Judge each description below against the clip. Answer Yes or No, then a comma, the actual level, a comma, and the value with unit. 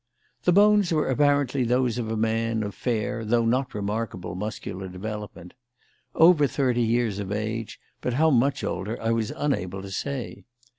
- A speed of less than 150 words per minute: No, average, 160 wpm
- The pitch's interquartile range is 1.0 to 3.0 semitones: No, average, 4.0 semitones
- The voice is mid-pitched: No, low, 115 Hz